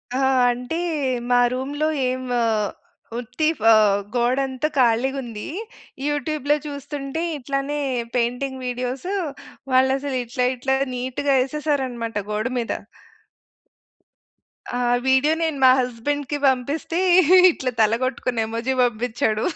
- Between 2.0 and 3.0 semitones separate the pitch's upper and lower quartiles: Yes, narrow, 2.5 semitones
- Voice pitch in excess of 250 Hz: Yes, very high, 260 Hz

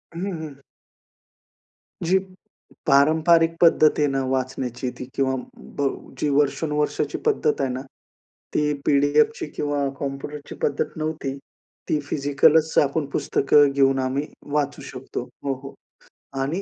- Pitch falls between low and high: Yes, medium, 145 Hz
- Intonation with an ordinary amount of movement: No, narrow, 1.9 semitones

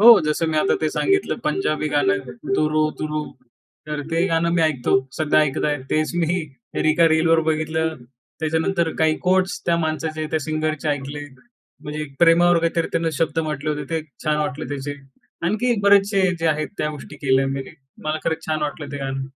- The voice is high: No, medium, 155 Hz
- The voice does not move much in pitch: Yes, narrow, 1.7 semitones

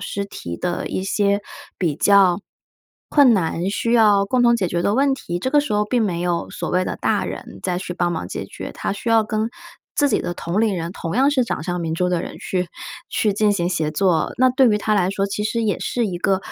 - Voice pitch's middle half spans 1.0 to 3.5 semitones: No, average, 4.1 semitones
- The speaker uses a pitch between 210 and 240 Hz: No, high, 200 Hz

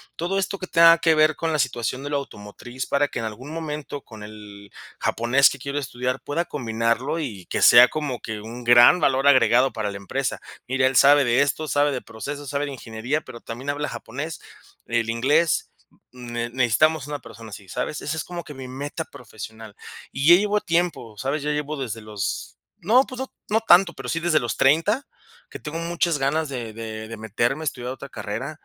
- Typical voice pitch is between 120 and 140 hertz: Yes, low, 135 Hz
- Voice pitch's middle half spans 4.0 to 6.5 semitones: Yes, average, 4.7 semitones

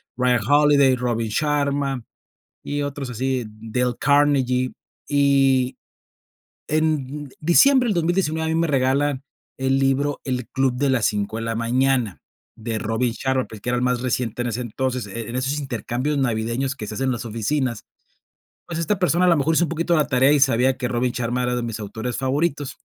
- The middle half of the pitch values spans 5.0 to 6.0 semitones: No, average, 3.0 semitones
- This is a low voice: Yes, low, 130 Hz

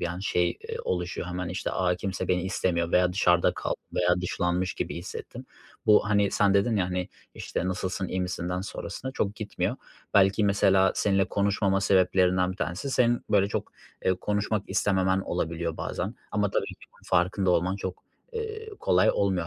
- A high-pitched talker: No, very low, 95 Hz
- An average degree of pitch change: No, narrow, 1.9 semitones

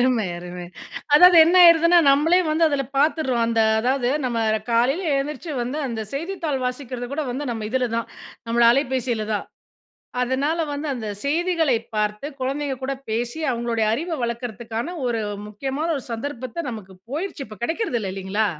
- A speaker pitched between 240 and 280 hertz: Yes, very high, 255 Hz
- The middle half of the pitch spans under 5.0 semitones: Yes, average, 4.4 semitones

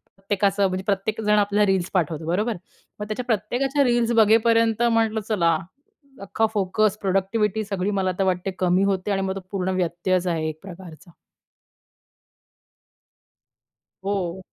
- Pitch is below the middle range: No, high, 195 Hz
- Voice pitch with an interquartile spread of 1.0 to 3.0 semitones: Yes, average, 2.7 semitones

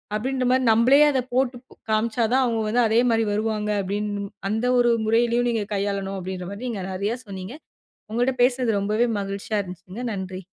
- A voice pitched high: Yes, high, 220 Hz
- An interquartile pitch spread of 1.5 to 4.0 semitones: Yes, average, 3.5 semitones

